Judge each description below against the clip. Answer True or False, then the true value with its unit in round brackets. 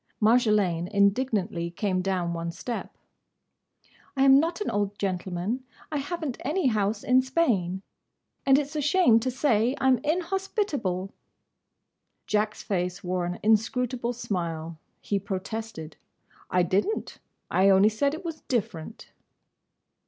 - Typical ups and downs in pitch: False (6.3 semitones)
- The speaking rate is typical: False (130 wpm)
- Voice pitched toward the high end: True (215 Hz)